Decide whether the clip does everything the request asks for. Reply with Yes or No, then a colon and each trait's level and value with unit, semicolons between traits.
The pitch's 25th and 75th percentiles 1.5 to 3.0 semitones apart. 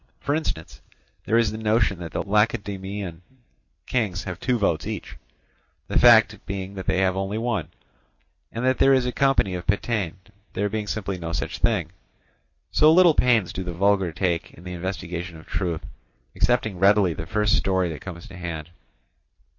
No: average, 3.8 semitones